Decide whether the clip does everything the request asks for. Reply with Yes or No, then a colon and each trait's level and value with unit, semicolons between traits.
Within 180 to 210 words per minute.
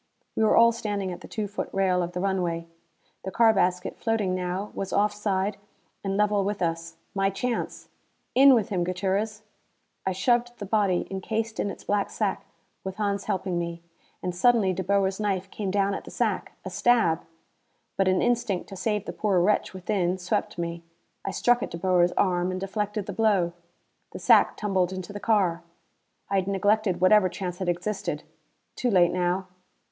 Yes: average, 185 wpm